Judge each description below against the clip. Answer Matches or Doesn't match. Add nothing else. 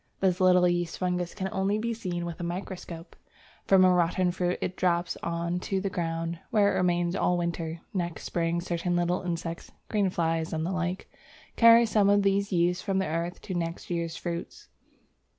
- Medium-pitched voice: Matches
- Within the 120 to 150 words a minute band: Doesn't match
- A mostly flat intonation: Matches